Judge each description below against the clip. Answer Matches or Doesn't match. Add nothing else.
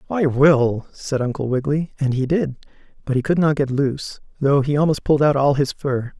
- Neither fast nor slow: Doesn't match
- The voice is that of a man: Matches